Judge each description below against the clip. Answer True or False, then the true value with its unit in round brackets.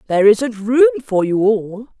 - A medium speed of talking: True (180 wpm)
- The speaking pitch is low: False (230 Hz)